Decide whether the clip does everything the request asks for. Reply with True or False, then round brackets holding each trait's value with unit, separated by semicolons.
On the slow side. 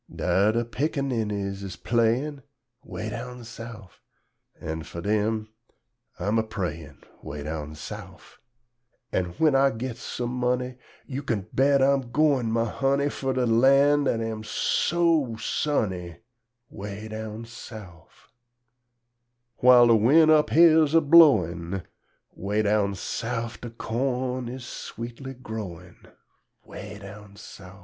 True (125 wpm)